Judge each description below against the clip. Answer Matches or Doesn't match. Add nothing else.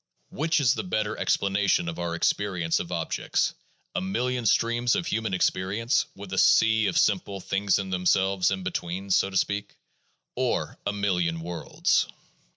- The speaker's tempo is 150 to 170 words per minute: Matches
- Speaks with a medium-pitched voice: Doesn't match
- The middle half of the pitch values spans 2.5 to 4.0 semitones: Matches